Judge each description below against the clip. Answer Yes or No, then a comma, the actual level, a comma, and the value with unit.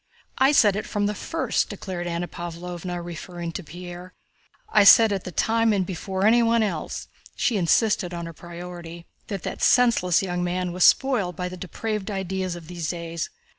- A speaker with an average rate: Yes, average, 170 wpm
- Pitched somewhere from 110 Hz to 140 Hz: No, medium, 180 Hz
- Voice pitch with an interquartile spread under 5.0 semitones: Yes, average, 3.0 semitones